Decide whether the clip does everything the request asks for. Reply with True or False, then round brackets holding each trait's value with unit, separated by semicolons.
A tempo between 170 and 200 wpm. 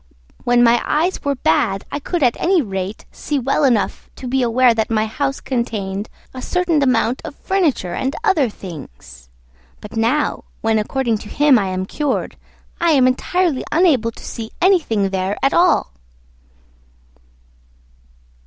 False (155 wpm)